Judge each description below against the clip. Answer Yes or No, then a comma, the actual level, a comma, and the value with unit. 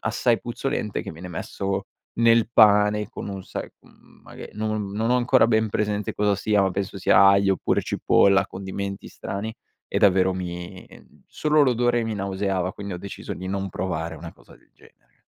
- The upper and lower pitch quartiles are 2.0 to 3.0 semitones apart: Yes, narrow, 2.4 semitones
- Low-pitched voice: Yes, low, 100 Hz